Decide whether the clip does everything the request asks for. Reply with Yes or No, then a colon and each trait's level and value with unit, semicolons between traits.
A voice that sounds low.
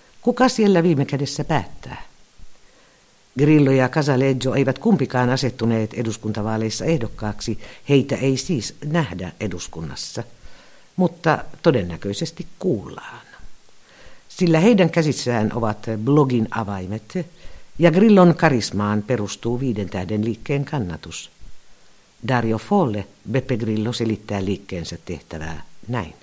Yes: low, 125 Hz